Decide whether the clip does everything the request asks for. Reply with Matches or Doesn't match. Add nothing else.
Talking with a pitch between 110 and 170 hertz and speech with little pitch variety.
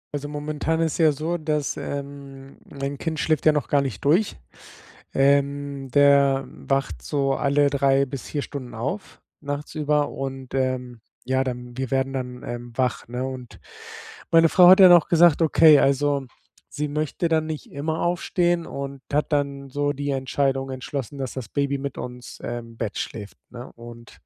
Matches